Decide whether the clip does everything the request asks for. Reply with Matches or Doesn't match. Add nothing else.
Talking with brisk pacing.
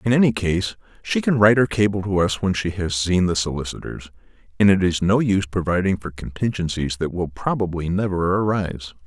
Doesn't match